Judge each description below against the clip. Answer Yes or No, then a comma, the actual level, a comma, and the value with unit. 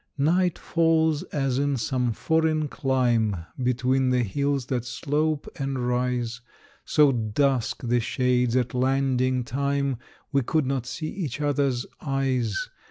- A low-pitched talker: Yes, low, 130 Hz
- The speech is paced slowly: Yes, slow, 130 wpm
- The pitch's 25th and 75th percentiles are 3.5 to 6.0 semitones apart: No, narrow, 2.5 semitones